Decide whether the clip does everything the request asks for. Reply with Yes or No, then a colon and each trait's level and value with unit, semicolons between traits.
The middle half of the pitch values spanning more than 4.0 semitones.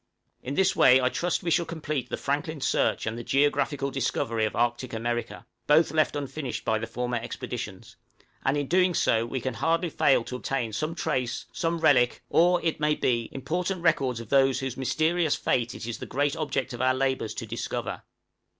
Yes: average, 4.6 semitones